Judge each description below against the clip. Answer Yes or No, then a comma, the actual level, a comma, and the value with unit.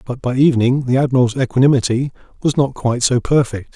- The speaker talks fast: No, average, 175 wpm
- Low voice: Yes, low, 130 Hz